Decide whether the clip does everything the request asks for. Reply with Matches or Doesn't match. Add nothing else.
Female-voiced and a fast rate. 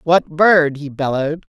Doesn't match